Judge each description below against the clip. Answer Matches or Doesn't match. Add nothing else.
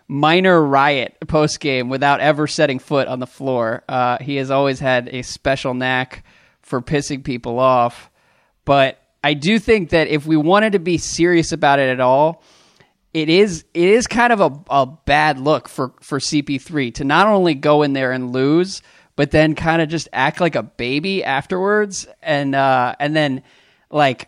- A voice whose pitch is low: Doesn't match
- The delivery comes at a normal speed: Matches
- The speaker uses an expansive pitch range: Doesn't match